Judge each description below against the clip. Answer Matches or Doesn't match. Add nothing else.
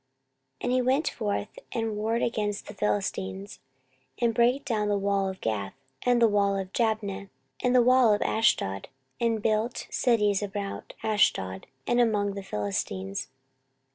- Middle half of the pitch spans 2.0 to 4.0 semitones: Matches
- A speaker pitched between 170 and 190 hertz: Doesn't match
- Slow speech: Doesn't match